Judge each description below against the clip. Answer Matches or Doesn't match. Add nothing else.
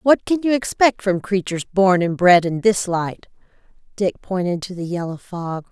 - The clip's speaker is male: Doesn't match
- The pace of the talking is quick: Doesn't match